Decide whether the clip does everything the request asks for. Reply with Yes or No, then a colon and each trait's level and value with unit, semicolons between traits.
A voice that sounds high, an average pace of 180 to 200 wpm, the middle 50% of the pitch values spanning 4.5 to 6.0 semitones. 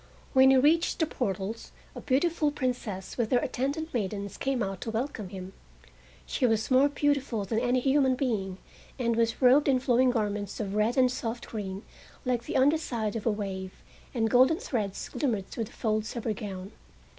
No: high, 235 Hz; average, 185 wpm; average, 4.1 semitones